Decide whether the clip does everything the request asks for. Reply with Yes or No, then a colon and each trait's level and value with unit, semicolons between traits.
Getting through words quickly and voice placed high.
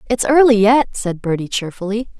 No: average, 165 wpm; high, 220 Hz